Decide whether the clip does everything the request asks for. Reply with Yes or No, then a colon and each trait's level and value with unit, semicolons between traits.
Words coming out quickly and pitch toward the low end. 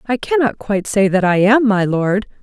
No: fast, 225 wpm; high, 210 Hz